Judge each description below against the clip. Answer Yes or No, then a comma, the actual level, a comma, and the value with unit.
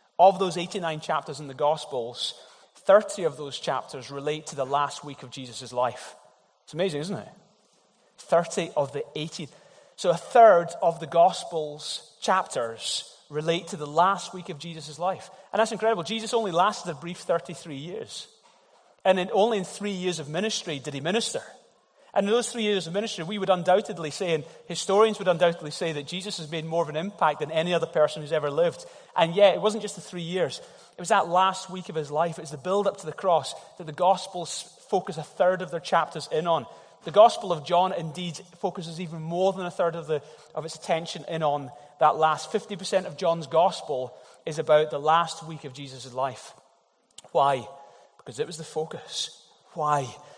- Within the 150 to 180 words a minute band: No, average, 200 wpm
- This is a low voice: No, medium, 170 Hz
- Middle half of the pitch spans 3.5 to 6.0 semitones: Yes, average, 3.9 semitones